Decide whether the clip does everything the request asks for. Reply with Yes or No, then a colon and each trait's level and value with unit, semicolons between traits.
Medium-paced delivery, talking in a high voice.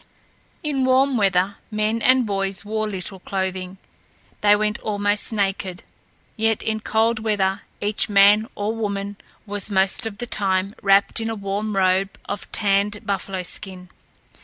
Yes: average, 145 wpm; high, 205 Hz